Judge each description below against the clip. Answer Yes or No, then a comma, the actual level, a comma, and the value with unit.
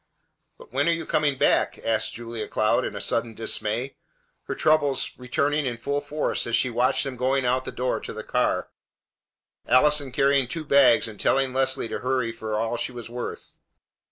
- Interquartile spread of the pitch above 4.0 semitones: No, average, 3.1 semitones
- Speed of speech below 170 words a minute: No, average, 185 wpm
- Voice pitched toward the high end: No, low, 130 Hz